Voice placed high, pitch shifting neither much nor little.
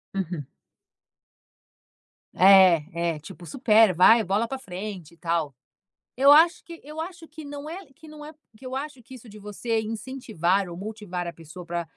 No: high, 215 Hz; wide, 7.5 semitones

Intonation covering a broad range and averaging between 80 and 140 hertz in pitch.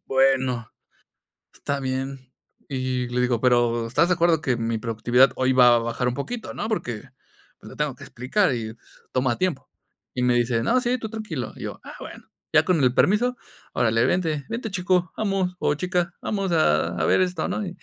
Yes: wide, 6.9 semitones; low, 135 Hz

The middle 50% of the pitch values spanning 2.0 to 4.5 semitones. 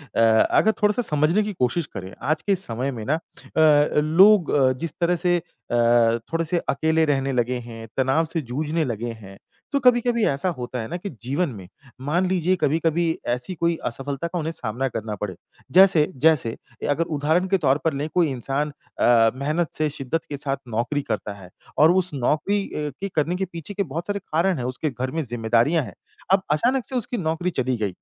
No: wide, 5.5 semitones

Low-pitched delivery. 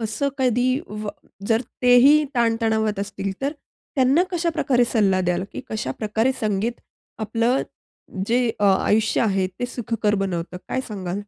No: high, 225 Hz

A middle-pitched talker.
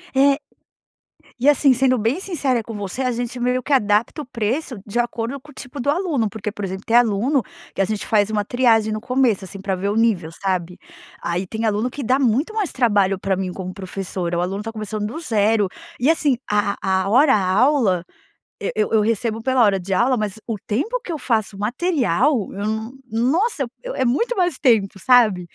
No: high, 225 Hz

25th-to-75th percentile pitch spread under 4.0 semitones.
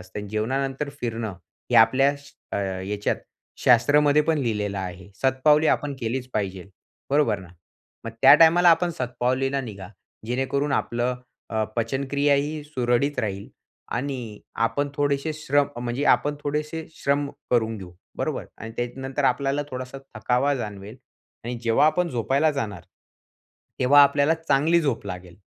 No: average, 4.3 semitones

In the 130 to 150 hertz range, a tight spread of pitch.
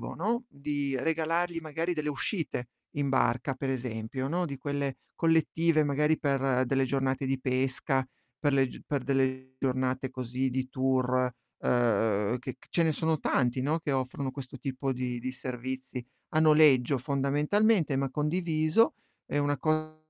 No: low, 135 Hz; average, 3.1 semitones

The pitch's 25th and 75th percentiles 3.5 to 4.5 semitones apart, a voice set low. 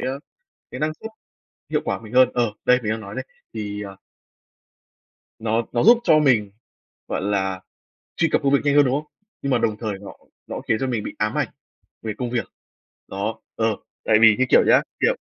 Yes: average, 3.9 semitones; low, 115 Hz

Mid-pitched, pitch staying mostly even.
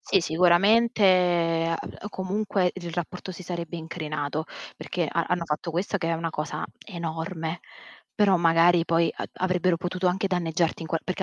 Yes: medium, 175 Hz; narrow, 1.9 semitones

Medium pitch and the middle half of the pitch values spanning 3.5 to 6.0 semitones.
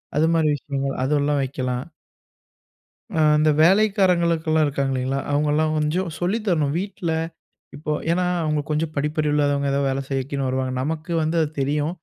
No: medium, 150 Hz; average, 2.7 semitones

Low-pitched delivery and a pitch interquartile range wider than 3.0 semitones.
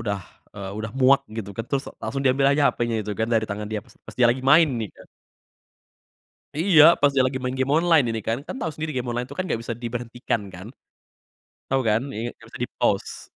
Yes: low, 125 Hz; average, 3.7 semitones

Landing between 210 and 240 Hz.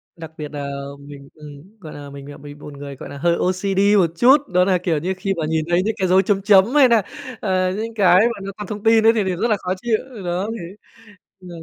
No: medium, 185 Hz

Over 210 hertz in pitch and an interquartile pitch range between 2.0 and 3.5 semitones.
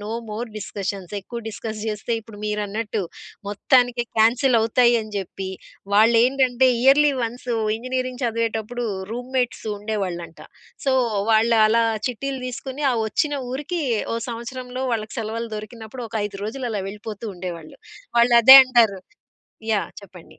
Yes: high, 230 Hz; average, 2.9 semitones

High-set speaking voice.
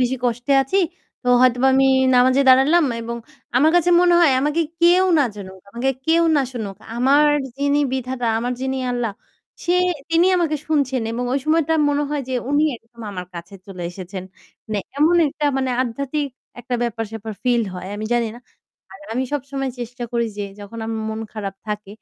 Yes: very high, 255 Hz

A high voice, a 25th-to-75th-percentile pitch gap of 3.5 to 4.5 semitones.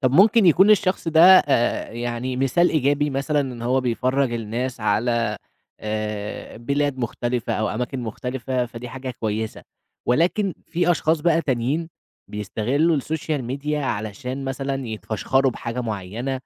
No: low, 130 Hz; average, 3.9 semitones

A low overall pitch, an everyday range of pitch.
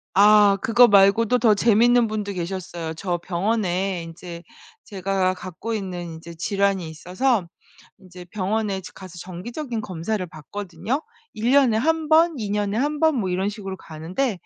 No: high, 200 Hz; average, 3.9 semitones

